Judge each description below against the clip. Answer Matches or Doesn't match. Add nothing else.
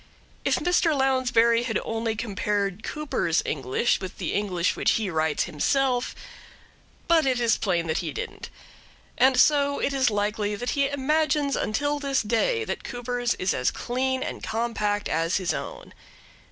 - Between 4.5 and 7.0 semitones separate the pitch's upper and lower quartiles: Matches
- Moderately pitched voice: Doesn't match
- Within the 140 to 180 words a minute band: Matches